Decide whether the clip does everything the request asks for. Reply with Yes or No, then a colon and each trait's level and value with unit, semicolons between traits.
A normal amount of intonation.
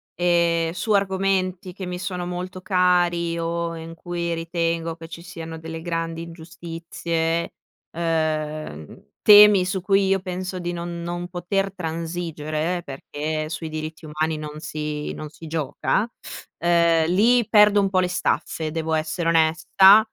No: narrow, 2.0 semitones